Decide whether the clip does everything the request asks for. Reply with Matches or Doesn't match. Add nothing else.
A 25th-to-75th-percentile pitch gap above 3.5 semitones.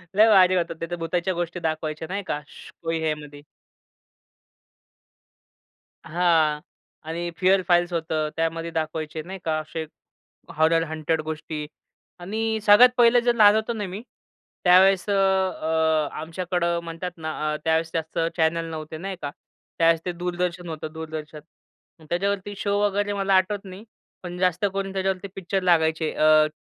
Doesn't match